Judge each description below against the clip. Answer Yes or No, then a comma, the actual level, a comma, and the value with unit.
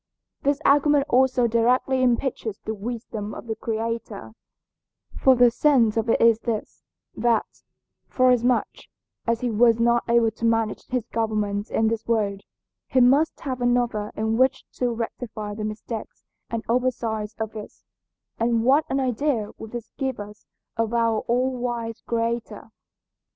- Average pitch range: No, narrow, 2.2 semitones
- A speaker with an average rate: Yes, average, 150 wpm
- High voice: Yes, high, 230 Hz